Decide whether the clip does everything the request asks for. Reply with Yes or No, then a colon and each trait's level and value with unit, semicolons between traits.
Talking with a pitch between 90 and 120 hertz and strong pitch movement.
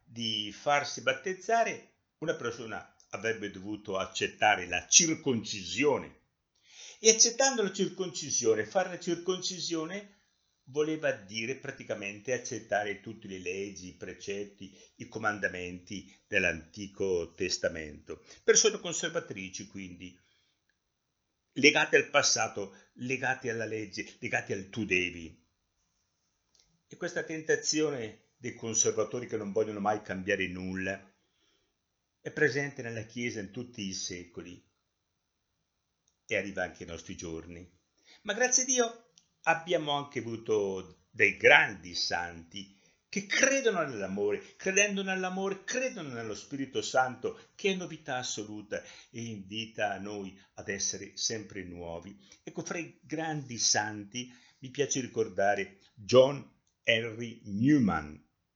Yes: low, 115 Hz; wide, 8.5 semitones